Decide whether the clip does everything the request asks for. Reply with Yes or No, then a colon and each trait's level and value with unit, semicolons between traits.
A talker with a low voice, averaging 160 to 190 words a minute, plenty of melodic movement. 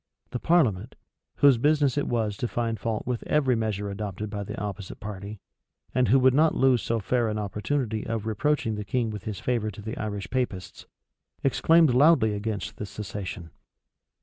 No: low, 110 Hz; average, 175 wpm; average, 3.7 semitones